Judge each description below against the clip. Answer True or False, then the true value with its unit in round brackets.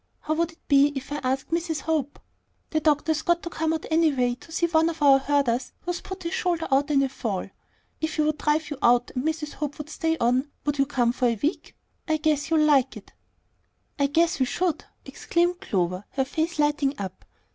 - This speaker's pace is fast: True (215 wpm)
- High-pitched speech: True (295 Hz)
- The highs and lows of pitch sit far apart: False (3.2 semitones)